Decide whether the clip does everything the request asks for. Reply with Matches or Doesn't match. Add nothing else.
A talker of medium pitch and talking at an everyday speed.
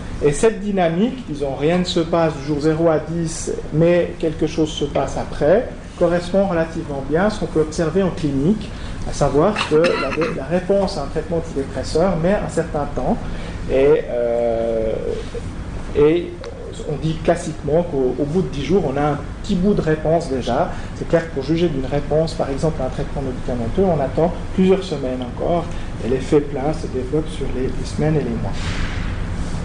Matches